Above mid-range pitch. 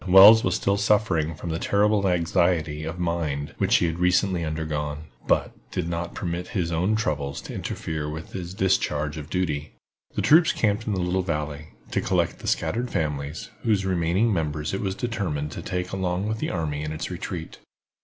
No: very low, 85 Hz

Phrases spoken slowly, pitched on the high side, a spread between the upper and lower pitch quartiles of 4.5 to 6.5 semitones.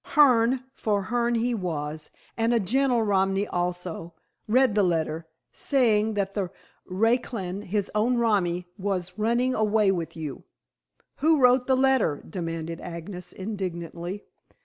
Yes: slow, 130 wpm; high, 205 Hz; average, 5.0 semitones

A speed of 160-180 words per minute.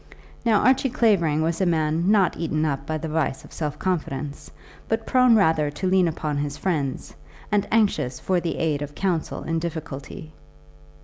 Yes: average, 175 wpm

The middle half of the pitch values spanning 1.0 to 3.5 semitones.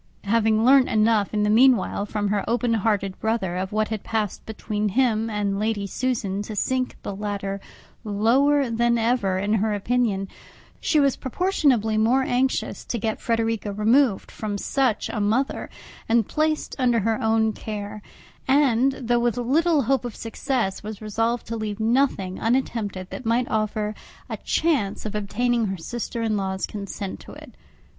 Yes: average, 2.9 semitones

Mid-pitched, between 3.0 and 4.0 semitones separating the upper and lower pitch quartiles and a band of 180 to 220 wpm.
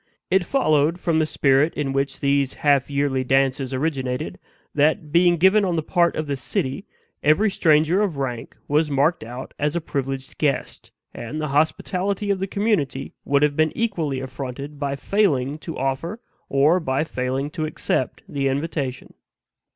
No: medium, 145 Hz; average, 3.6 semitones; average, 165 wpm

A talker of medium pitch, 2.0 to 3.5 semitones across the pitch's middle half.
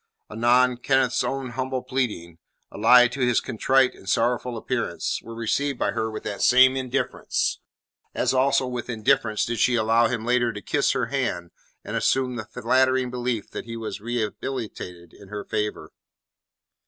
No: low, 120 Hz; narrow, 2.6 semitones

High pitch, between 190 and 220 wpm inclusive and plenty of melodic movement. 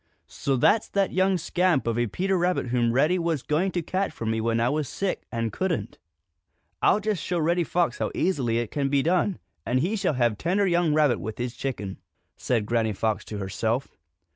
No: medium, 145 Hz; fast, 205 wpm; wide, 7.4 semitones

